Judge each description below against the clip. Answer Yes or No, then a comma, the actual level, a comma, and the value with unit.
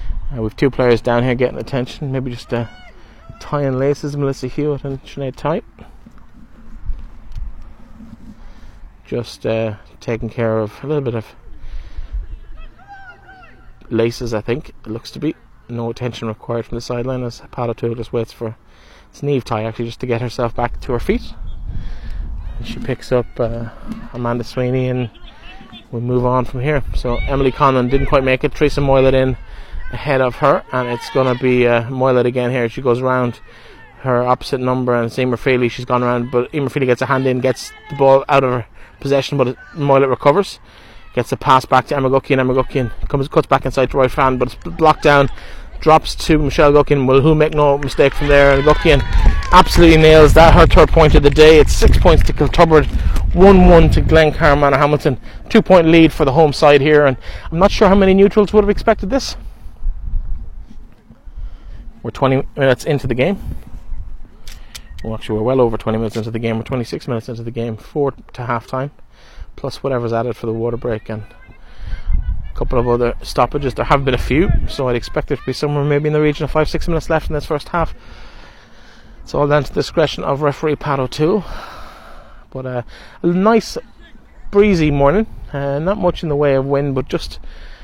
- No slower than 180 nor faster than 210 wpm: Yes, average, 190 wpm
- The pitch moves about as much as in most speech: Yes, average, 3.7 semitones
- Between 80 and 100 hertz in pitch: No, low, 130 Hz